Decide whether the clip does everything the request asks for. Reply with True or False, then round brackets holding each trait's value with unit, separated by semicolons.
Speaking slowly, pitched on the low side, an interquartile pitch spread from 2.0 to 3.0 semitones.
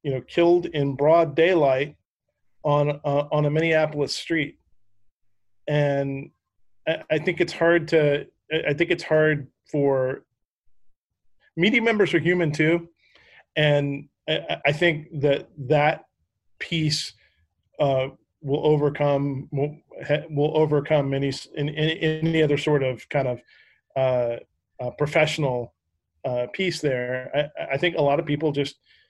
False (130 wpm; 145 Hz; 2.7 semitones)